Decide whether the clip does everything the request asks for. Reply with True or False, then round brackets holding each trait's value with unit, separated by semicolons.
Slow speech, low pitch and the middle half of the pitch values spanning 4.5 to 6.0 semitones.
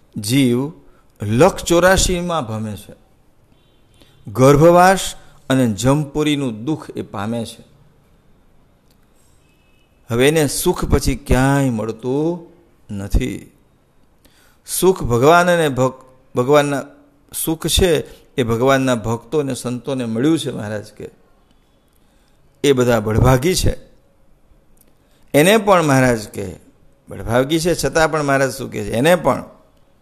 True (105 wpm; 130 Hz; 4.8 semitones)